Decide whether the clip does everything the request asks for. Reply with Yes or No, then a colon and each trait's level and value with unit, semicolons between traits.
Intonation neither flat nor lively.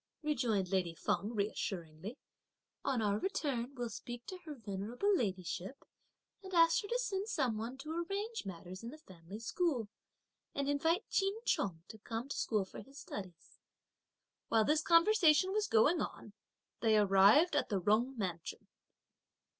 No: wide, 8.2 semitones